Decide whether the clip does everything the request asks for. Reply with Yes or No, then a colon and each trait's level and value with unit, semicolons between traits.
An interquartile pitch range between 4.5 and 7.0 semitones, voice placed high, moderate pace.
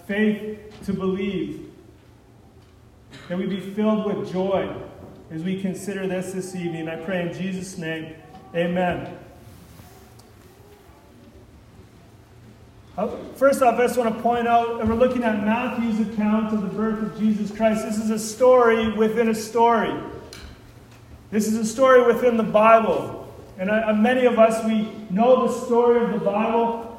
Yes: average, 5.2 semitones; high, 210 Hz; average, 150 wpm